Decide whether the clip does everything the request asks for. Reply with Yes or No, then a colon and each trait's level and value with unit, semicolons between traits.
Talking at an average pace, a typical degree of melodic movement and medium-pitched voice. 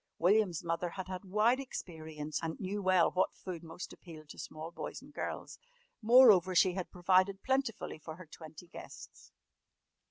Yes: average, 160 wpm; average, 3.2 semitones; medium, 180 Hz